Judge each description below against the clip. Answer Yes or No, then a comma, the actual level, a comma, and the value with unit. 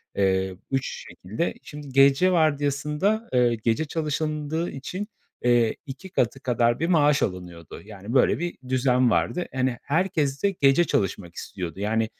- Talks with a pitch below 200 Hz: Yes, low, 135 Hz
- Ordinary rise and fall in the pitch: No, wide, 5.7 semitones